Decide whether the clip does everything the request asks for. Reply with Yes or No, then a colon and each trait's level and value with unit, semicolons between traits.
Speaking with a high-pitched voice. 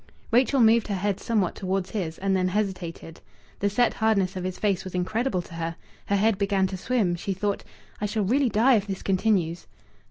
Yes: high, 195 Hz